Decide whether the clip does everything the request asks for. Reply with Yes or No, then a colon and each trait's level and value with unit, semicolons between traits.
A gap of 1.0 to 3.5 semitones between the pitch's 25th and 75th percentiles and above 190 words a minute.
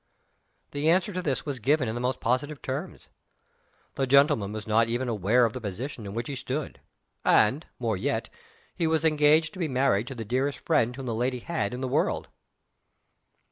No: average, 4.1 semitones; average, 200 wpm